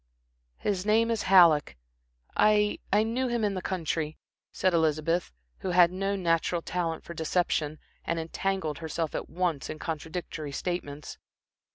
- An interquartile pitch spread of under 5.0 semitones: Yes, average, 3.4 semitones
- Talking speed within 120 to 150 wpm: Yes, average, 145 wpm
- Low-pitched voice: No, medium, 175 Hz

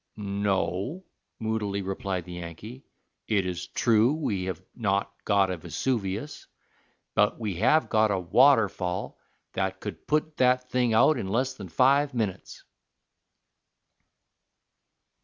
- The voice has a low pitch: Yes, low, 105 Hz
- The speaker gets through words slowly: Yes, slow, 120 wpm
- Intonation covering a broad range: No, average, 4.9 semitones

